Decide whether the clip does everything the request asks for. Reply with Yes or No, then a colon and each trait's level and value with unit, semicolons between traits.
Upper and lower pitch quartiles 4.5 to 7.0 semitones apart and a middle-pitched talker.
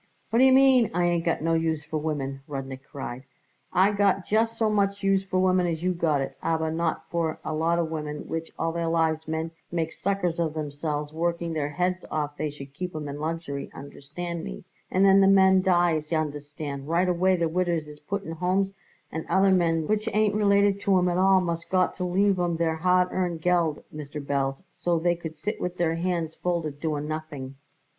No: average, 3.1 semitones; medium, 170 Hz